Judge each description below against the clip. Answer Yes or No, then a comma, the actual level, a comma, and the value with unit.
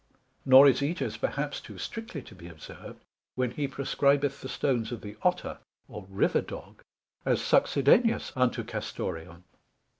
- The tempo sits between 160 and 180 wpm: No, average, 145 wpm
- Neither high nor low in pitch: No, low, 130 Hz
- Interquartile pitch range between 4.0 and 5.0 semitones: No, wide, 5.4 semitones